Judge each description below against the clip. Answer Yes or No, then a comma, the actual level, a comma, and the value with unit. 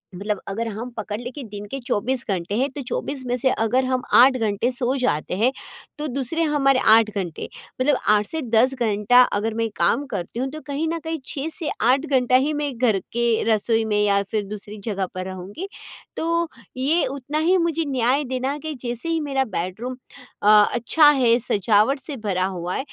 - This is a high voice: Yes, high, 245 Hz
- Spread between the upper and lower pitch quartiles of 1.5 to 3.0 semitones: No, average, 4.7 semitones